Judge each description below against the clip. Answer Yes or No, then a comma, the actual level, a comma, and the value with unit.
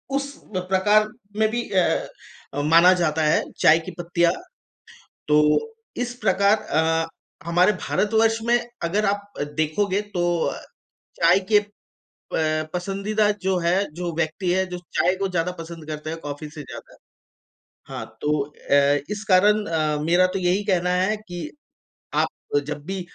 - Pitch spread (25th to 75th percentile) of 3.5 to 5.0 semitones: Yes, average, 3.9 semitones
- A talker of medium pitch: Yes, medium, 180 Hz